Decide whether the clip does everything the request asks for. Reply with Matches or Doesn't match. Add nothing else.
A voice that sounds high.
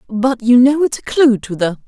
Matches